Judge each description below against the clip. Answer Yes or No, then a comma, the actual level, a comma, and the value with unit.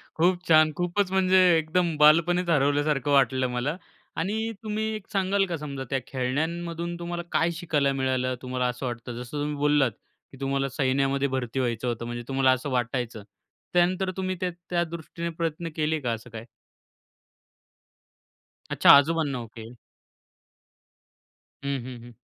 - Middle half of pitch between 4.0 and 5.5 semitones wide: Yes, average, 4.9 semitones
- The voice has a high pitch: No, medium, 145 Hz